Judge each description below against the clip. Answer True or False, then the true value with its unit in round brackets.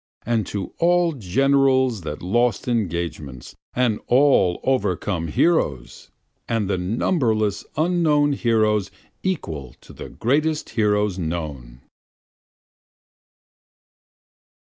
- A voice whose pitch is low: True (110 Hz)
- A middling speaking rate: False (90 wpm)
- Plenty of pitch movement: True (7.5 semitones)